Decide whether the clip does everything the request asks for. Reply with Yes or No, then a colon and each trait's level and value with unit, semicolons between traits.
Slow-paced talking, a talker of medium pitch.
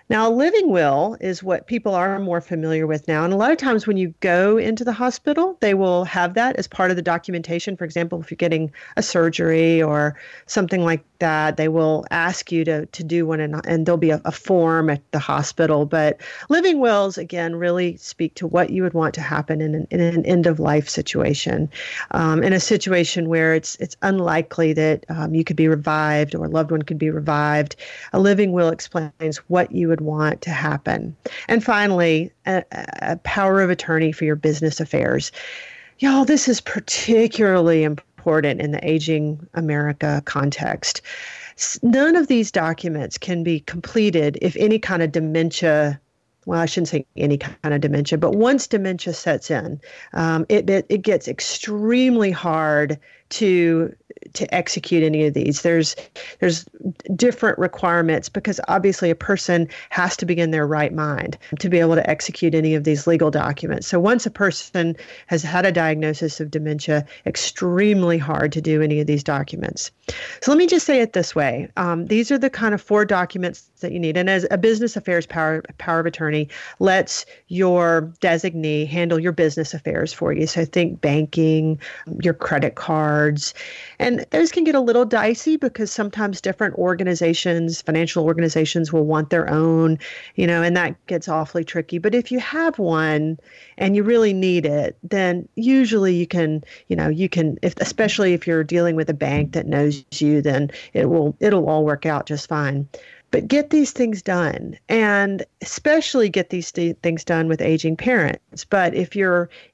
No: average, 185 wpm; medium, 170 Hz